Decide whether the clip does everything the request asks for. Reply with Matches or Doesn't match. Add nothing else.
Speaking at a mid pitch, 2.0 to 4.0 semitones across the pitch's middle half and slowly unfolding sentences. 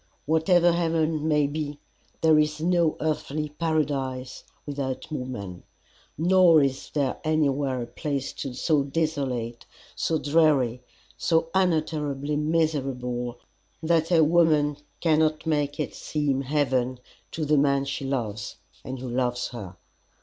Matches